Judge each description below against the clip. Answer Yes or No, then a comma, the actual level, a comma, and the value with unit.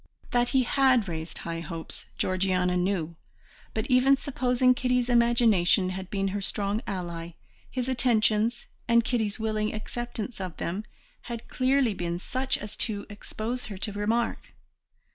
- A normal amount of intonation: Yes, average, 4.6 semitones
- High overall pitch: Yes, high, 215 Hz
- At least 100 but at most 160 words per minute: Yes, average, 145 wpm